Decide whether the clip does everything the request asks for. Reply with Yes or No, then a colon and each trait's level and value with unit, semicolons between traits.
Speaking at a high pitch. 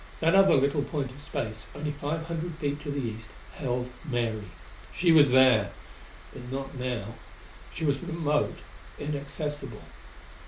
No: medium, 140 Hz